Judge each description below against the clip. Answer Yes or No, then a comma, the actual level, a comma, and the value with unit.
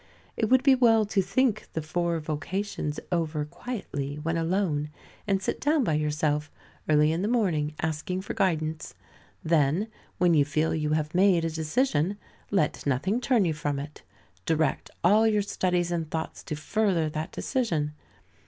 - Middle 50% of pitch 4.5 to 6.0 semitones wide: Yes, average, 4.8 semitones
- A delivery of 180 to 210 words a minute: No, average, 160 wpm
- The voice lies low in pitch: No, medium, 165 Hz